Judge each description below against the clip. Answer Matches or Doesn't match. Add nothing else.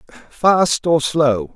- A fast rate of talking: Doesn't match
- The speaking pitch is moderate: Matches